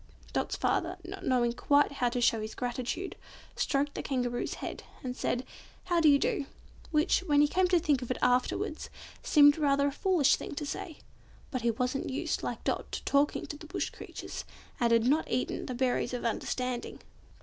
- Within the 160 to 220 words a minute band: Yes, average, 190 wpm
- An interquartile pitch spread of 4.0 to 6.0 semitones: No, average, 3.4 semitones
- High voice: Yes, very high, 275 Hz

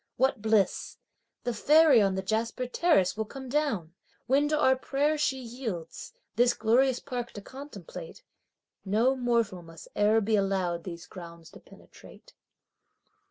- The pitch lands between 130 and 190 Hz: No, high, 235 Hz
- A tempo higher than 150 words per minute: No, average, 145 wpm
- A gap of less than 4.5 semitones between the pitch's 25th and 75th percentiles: No, wide, 5.4 semitones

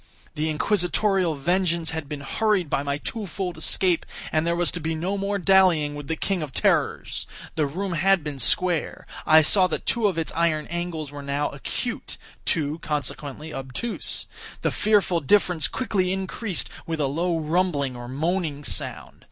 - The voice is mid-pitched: Yes, medium, 165 Hz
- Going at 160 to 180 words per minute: Yes, average, 170 wpm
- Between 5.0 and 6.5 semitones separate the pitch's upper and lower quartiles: No, average, 3.9 semitones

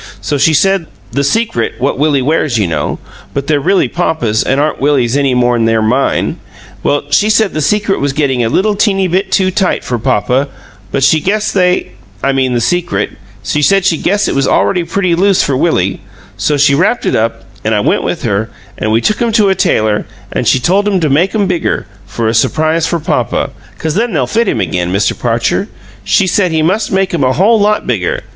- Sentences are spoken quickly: Yes, fast, 220 wpm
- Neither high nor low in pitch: Yes, medium, 155 Hz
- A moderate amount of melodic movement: No, wide, 7.4 semitones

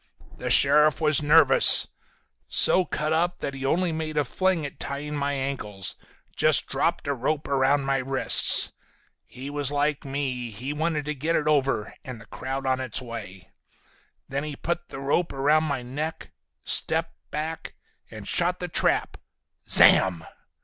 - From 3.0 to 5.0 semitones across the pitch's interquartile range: No, narrow, 2.6 semitones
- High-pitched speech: No, medium, 145 Hz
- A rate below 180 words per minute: Yes, average, 160 wpm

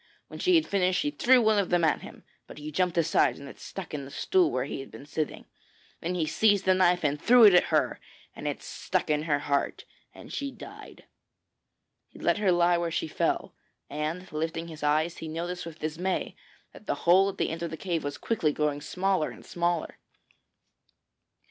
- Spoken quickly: Yes, fast, 210 wpm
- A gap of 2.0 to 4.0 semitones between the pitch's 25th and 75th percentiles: Yes, average, 3.6 semitones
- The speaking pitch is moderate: Yes, medium, 170 Hz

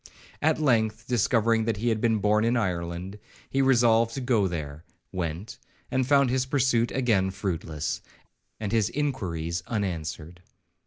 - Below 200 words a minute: Yes, average, 140 wpm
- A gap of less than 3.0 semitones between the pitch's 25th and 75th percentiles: No, average, 5.2 semitones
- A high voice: No, low, 110 Hz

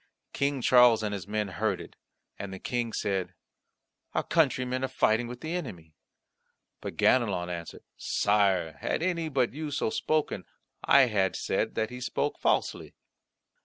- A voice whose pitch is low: Yes, low, 120 Hz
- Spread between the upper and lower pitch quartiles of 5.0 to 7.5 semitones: Yes, wide, 5.5 semitones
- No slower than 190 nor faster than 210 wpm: No, average, 155 wpm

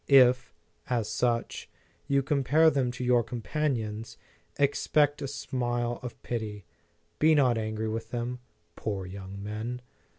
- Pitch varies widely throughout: No, average, 3.5 semitones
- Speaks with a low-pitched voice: Yes, low, 120 Hz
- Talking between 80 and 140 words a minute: Yes, slow, 135 wpm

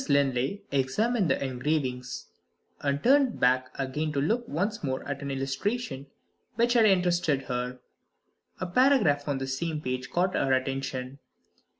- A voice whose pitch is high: No, medium, 140 Hz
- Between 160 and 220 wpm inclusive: No, average, 140 wpm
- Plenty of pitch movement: Yes, wide, 5.9 semitones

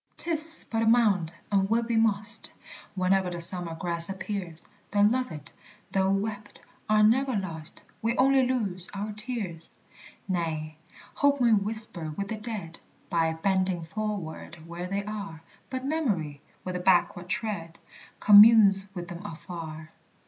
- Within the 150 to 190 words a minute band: No, average, 140 wpm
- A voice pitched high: Yes, high, 195 Hz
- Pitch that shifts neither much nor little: Yes, average, 4.4 semitones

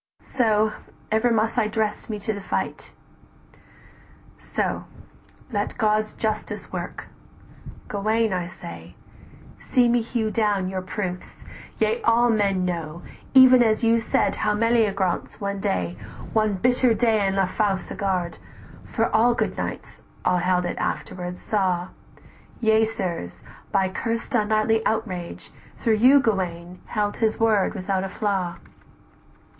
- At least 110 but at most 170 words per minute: Yes, slow, 135 wpm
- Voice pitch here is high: Yes, high, 210 Hz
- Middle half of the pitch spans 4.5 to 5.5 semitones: No, average, 3.2 semitones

